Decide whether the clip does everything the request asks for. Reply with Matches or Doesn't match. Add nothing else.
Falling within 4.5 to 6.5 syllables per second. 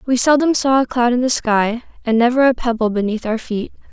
Matches